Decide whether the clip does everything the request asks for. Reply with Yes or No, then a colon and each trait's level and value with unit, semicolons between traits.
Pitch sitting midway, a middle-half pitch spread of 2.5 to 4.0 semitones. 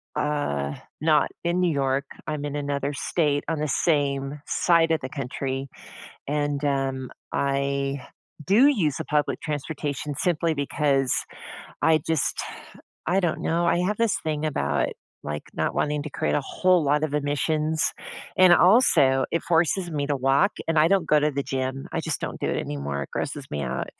Yes: medium, 145 Hz; average, 2.9 semitones